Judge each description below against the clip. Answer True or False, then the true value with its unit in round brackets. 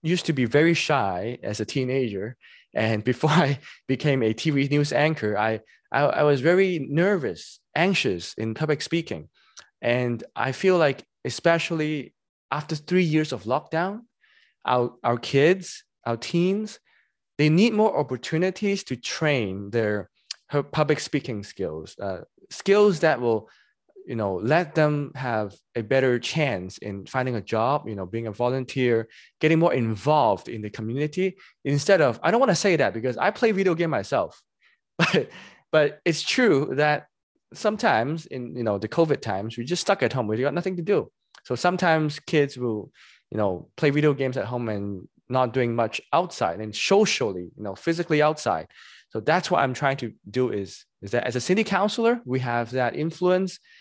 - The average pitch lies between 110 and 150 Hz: True (140 Hz)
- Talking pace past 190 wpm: False (175 wpm)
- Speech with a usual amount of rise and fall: False (6.1 semitones)